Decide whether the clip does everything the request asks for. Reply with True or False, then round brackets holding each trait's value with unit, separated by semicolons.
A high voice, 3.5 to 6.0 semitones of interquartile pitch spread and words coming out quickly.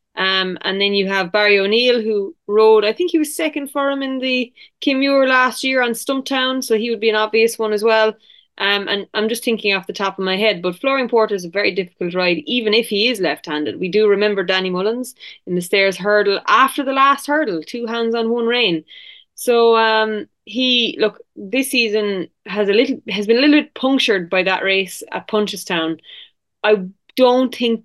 True (220 Hz; 4.1 semitones; 210 wpm)